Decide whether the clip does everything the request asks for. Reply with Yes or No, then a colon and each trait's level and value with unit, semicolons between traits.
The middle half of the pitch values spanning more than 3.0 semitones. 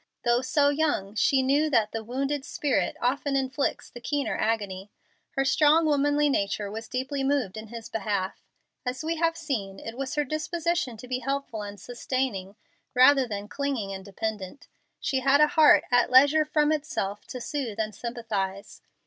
Yes: average, 4.9 semitones